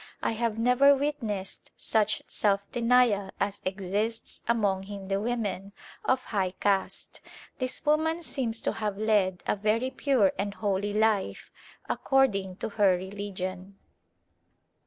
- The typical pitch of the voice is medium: No, high, 210 Hz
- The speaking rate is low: Yes, slow, 125 wpm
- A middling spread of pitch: Yes, average, 3.2 semitones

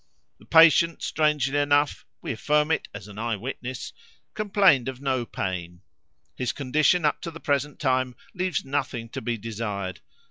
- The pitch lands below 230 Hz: Yes, low, 135 Hz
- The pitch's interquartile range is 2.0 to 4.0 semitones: No, average, 4.6 semitones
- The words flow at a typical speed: Yes, average, 155 wpm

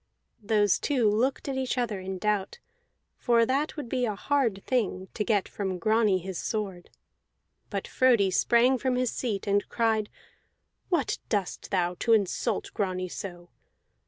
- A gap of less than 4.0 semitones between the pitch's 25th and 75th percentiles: No, average, 4.3 semitones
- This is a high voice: Yes, high, 215 Hz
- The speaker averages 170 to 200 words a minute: No, average, 160 wpm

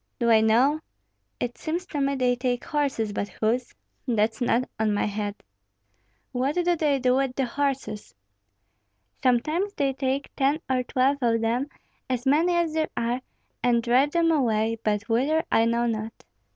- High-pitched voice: Yes, very high, 255 Hz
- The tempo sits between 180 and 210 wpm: No, average, 165 wpm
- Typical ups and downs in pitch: Yes, average, 3.8 semitones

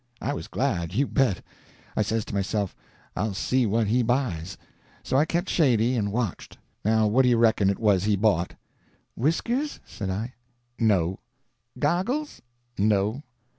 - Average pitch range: Yes, average, 4.7 semitones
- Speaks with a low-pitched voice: Yes, low, 110 Hz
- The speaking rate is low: No, average, 155 wpm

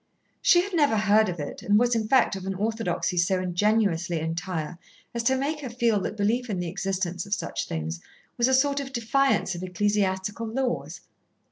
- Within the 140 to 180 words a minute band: No, average, 195 wpm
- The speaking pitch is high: Yes, high, 205 Hz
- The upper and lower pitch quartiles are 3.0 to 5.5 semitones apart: Yes, average, 4.8 semitones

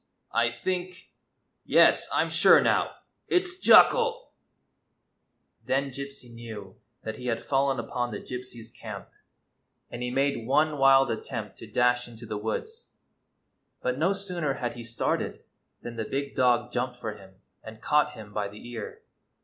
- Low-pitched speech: Yes, low, 125 Hz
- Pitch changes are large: No, average, 3.5 semitones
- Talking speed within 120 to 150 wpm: No, average, 165 wpm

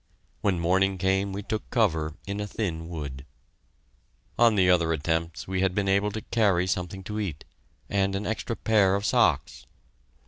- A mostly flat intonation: No, average, 3.5 semitones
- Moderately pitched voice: No, very low, 95 Hz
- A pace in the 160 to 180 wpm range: Yes, average, 170 wpm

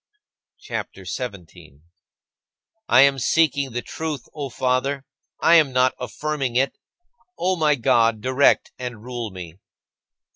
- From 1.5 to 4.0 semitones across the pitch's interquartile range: Yes, average, 2.9 semitones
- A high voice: No, low, 130 Hz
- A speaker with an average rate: No, slow, 130 wpm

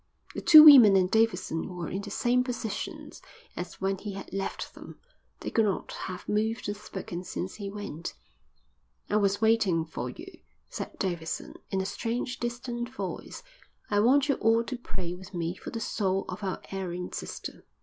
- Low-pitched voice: No, high, 205 Hz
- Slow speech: No, average, 180 wpm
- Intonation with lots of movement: No, average, 3.8 semitones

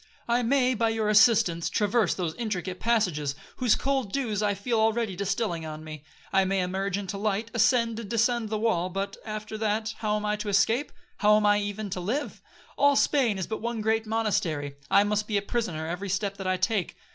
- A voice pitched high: Yes, high, 210 Hz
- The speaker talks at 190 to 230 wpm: Yes, average, 200 wpm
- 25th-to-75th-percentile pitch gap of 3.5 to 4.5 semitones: No, average, 2.8 semitones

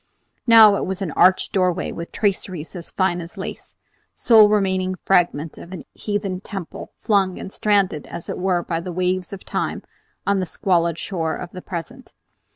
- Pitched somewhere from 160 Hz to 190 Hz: Yes, medium, 185 Hz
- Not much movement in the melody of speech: Yes, narrow, 2.3 semitones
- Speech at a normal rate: Yes, average, 175 wpm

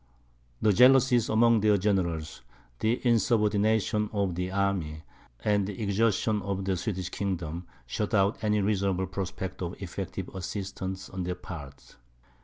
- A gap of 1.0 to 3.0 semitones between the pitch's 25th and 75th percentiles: Yes, narrow, 2.5 semitones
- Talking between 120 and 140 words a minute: Yes, slow, 135 wpm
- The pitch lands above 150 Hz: No, low, 100 Hz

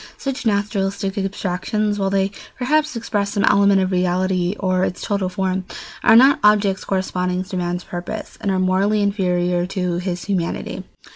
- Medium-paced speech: Yes, average, 155 wpm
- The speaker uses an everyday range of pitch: No, narrow, 2.0 semitones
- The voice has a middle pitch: No, high, 195 Hz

